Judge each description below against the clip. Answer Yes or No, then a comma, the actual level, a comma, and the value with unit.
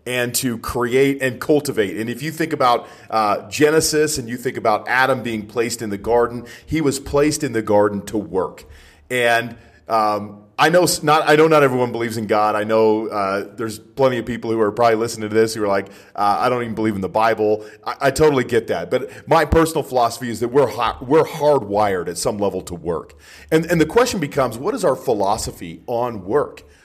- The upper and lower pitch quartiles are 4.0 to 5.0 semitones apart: Yes, average, 4.5 semitones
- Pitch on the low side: Yes, low, 120 Hz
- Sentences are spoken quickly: Yes, fast, 215 wpm